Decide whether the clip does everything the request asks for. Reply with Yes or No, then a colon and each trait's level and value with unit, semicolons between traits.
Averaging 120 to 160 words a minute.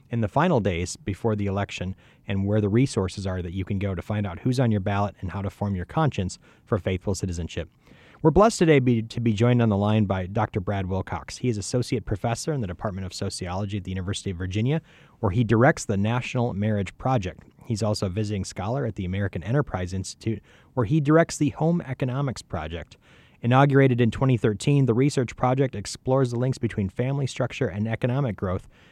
No: fast, 205 wpm